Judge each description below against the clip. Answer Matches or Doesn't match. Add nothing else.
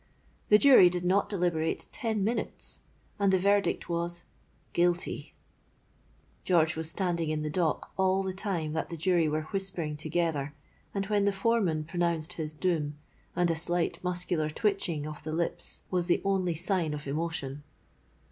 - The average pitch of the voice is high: Doesn't match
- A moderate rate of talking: Matches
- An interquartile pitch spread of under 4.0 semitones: Matches